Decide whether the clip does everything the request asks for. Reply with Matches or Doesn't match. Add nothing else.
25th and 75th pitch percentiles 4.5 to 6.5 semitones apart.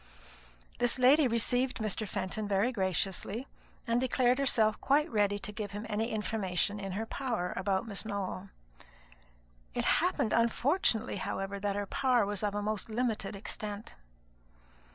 Doesn't match